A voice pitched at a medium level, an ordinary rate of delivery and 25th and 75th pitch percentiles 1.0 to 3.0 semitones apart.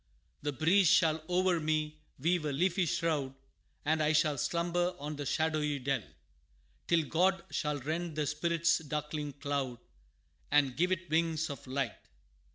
Yes: medium, 155 Hz; average, 150 wpm; narrow, 2.6 semitones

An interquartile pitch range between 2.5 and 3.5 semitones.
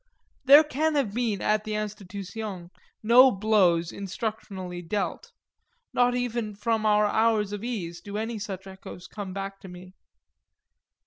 Yes: average, 2.9 semitones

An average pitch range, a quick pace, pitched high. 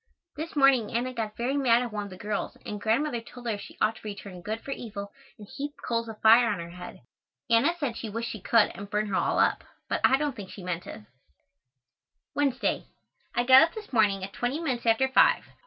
Yes: average, 4.1 semitones; fast, 225 wpm; high, 230 Hz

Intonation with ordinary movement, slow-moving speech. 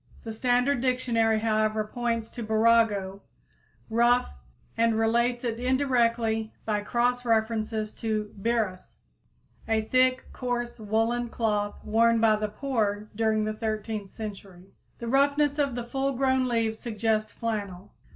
No: narrow, 2.1 semitones; slow, 130 wpm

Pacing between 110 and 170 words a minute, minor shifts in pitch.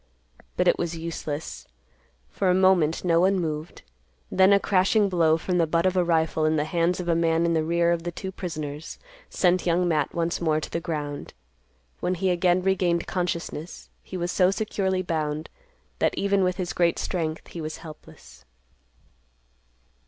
No: average, 180 wpm; narrow, 2.2 semitones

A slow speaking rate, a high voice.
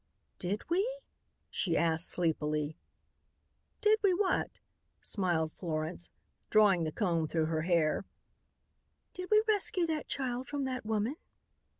Yes: slow, 120 wpm; high, 200 Hz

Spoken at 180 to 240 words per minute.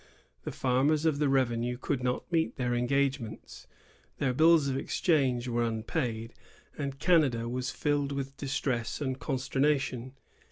No: average, 145 wpm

